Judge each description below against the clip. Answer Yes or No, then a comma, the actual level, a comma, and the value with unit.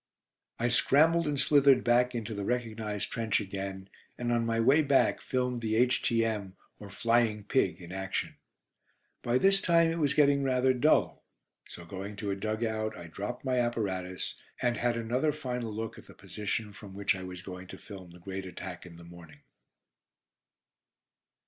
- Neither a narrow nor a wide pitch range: Yes, average, 4.4 semitones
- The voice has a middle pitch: No, low, 115 Hz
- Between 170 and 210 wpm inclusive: Yes, average, 175 wpm